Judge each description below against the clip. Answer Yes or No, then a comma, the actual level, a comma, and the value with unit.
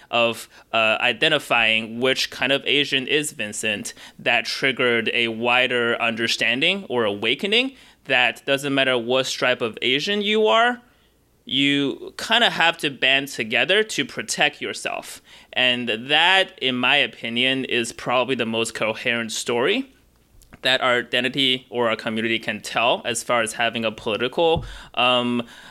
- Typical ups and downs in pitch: Yes, average, 3.3 semitones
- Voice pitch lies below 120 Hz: No, low, 125 Hz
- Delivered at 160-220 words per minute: No, average, 140 wpm